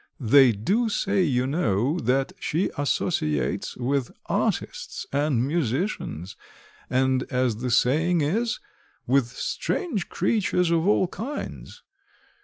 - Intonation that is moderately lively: No, wide, 6.2 semitones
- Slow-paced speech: Yes, slow, 110 wpm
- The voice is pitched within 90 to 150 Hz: Yes, medium, 140 Hz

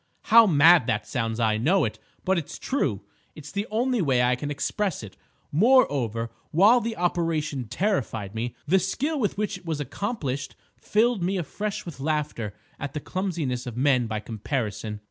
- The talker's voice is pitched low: No, medium, 150 Hz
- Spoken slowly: No, average, 170 wpm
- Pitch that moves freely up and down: Yes, wide, 8.1 semitones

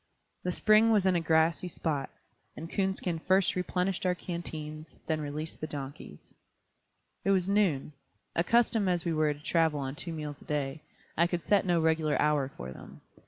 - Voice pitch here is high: No, medium, 165 Hz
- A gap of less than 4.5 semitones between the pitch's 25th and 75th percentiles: Yes, average, 3.3 semitones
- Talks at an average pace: Yes, average, 175 wpm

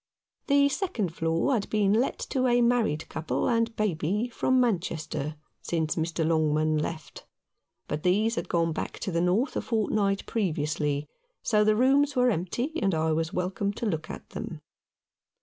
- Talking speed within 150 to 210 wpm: Yes, average, 165 wpm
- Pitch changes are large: Yes, wide, 6.3 semitones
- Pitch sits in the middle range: No, high, 195 Hz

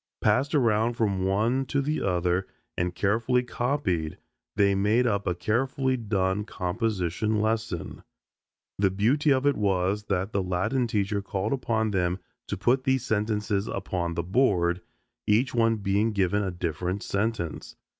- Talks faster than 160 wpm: No, average, 145 wpm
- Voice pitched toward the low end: Yes, low, 105 Hz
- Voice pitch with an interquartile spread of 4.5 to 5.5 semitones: No, average, 3.8 semitones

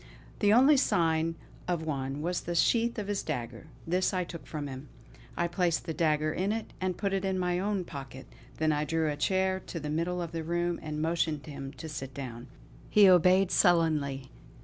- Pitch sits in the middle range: Yes, medium, 165 Hz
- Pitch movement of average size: Yes, average, 3.6 semitones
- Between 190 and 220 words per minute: Yes, average, 200 wpm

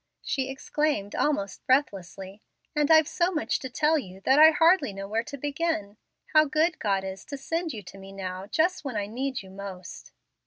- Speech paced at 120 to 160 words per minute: No, average, 195 wpm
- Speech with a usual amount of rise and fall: No, wide, 7.7 semitones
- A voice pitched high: Yes, very high, 265 Hz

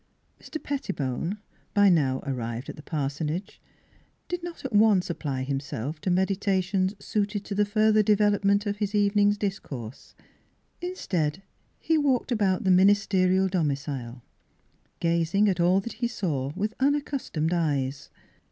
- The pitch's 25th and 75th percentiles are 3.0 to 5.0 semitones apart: No, wide, 5.5 semitones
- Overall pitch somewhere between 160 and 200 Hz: Yes, high, 190 Hz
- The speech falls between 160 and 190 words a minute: No, average, 150 wpm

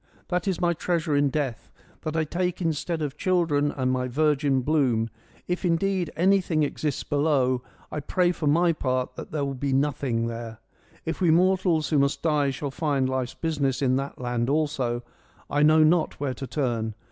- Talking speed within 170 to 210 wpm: Yes, average, 180 wpm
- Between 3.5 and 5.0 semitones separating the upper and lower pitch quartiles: Yes, average, 3.9 semitones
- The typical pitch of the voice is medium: Yes, medium, 145 Hz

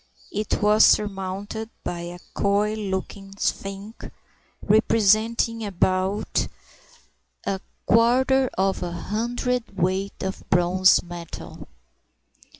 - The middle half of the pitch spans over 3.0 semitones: No, narrow, 2.6 semitones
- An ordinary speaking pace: No, slow, 85 wpm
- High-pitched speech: Yes, high, 200 Hz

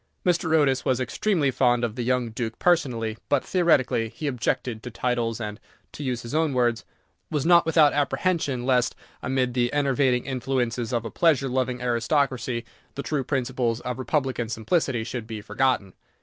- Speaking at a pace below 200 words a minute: Yes, average, 165 wpm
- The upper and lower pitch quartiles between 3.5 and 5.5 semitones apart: No, average, 3.0 semitones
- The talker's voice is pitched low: Yes, low, 125 Hz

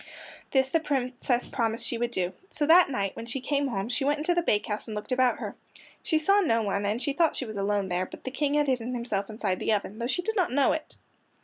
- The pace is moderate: No, fast, 255 wpm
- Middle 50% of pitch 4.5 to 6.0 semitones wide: Yes, wide, 5.4 semitones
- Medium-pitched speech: No, very high, 250 Hz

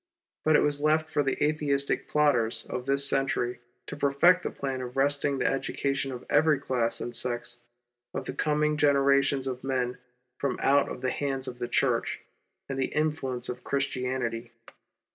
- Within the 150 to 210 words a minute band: Yes, average, 170 wpm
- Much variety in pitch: No, narrow, 2.4 semitones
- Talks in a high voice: No, low, 135 Hz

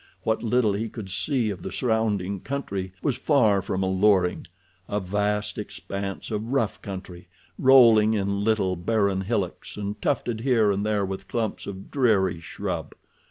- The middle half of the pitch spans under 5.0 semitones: Yes, average, 2.8 semitones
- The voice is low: Yes, low, 105 Hz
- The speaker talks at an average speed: Yes, average, 150 wpm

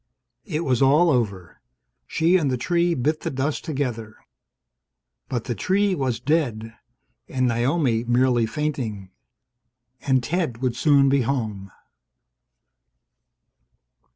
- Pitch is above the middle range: No, low, 130 Hz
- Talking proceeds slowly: Yes, slow, 115 wpm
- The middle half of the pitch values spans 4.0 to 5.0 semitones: Yes, average, 4.7 semitones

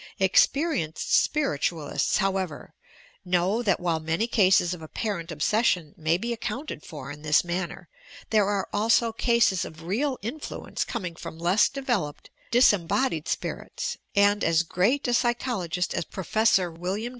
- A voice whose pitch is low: No, high, 190 Hz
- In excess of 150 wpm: No, average, 145 wpm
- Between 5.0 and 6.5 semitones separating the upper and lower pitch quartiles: Yes, wide, 5.6 semitones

